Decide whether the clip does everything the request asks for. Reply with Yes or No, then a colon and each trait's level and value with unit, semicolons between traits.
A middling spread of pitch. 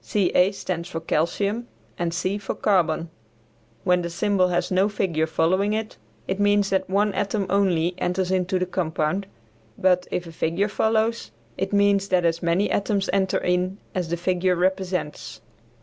No: narrow, 2.3 semitones